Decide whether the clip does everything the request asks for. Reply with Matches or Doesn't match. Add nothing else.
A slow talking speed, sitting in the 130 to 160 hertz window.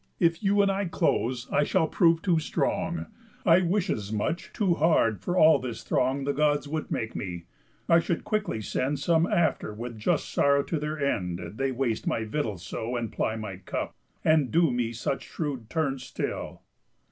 Doesn't match